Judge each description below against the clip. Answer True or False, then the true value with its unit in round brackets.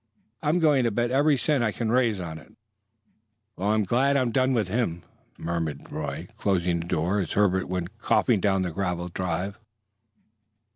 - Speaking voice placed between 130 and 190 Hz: False (100 Hz)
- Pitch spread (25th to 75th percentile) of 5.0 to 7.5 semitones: True (5.4 semitones)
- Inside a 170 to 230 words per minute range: True (175 wpm)